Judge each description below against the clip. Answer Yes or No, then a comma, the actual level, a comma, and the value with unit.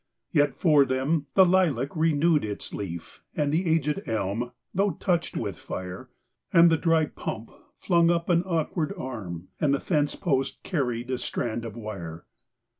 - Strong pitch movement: Yes, wide, 6.3 semitones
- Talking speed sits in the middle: Yes, average, 160 wpm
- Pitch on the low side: No, medium, 145 Hz